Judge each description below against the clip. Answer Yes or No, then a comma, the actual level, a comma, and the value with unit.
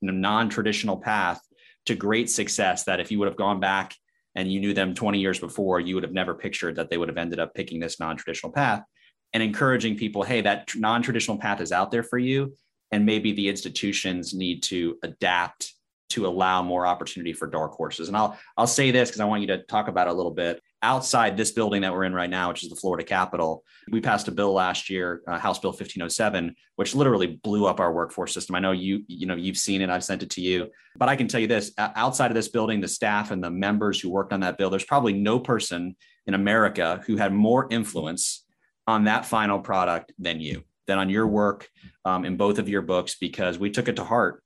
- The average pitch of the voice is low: Yes, low, 100 Hz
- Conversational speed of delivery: No, fast, 230 wpm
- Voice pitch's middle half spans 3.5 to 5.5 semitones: No, average, 3.0 semitones